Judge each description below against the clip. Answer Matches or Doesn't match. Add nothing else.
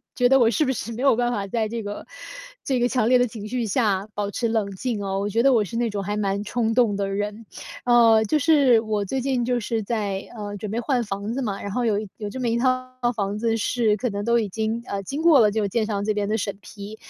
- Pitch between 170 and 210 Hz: Doesn't match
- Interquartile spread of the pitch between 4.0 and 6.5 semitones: Doesn't match